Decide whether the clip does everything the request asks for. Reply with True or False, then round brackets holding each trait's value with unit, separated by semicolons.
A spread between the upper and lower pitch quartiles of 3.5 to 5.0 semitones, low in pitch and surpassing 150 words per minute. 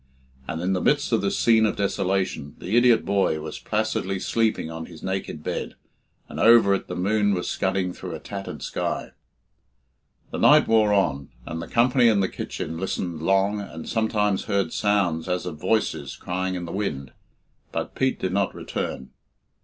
False (3.1 semitones; 95 Hz; 175 wpm)